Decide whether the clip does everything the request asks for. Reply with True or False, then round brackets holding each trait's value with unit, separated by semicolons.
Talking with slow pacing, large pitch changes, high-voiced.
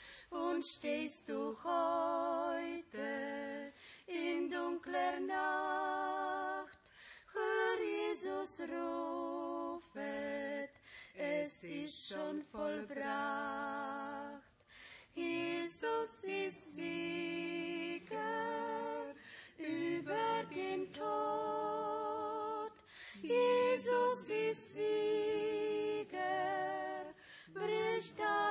True (55 wpm; 6.0 semitones; 335 Hz)